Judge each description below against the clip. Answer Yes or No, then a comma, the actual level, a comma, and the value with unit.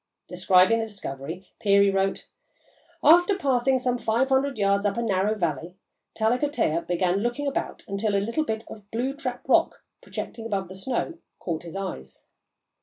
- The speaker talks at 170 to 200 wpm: No, average, 155 wpm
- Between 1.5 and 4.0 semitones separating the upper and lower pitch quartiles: No, average, 4.7 semitones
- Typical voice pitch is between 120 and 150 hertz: No, high, 210 Hz